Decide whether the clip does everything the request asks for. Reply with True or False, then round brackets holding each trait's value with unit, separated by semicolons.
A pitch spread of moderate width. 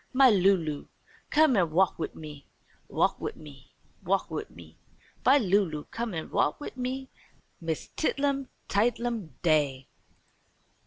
False (8.4 semitones)